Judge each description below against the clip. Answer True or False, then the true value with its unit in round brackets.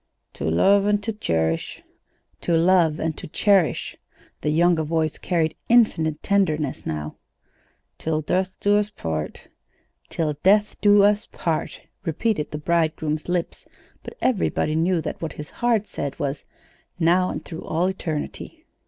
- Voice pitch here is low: False (165 Hz)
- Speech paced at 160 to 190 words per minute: False (145 wpm)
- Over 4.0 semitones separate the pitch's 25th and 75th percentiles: True (4.5 semitones)